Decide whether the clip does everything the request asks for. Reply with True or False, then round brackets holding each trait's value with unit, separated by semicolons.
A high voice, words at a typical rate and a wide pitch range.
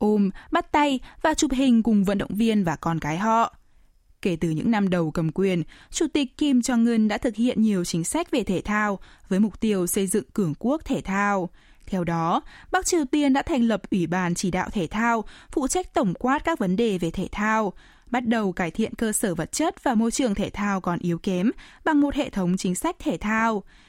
True (215 Hz; 230 wpm; 6.0 semitones)